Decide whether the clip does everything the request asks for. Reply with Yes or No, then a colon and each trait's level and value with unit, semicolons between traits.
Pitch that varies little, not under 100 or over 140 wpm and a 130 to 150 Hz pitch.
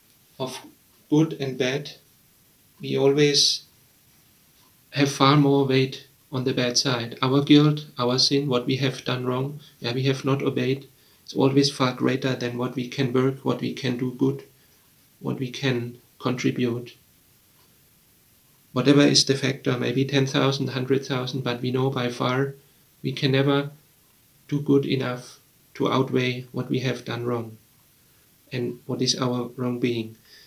No: narrow, 1.8 semitones; average, 150 wpm; low, 135 Hz